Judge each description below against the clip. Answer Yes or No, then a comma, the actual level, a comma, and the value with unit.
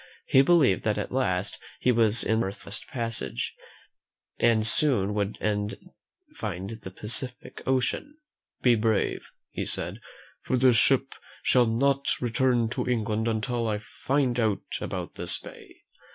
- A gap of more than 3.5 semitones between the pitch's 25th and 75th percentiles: No, average, 3.2 semitones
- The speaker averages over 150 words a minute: No, average, 140 wpm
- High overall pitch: No, low, 115 Hz